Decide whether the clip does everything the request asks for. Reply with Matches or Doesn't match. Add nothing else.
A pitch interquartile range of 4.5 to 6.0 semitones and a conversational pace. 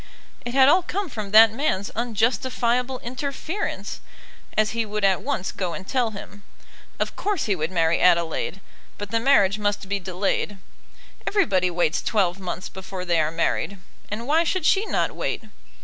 Matches